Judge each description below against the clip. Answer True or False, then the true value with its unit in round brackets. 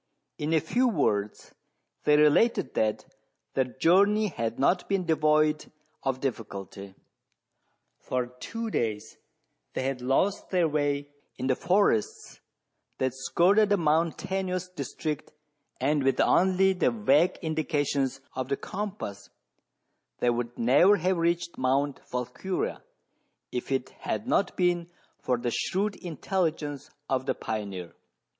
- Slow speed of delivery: True (125 wpm)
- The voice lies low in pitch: False (150 Hz)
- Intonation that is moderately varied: False (6.1 semitones)